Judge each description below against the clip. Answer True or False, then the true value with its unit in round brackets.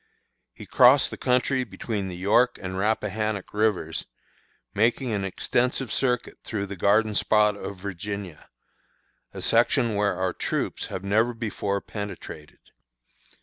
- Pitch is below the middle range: True (105 Hz)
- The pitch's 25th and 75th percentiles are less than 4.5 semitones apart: True (2.8 semitones)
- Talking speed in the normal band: False (130 wpm)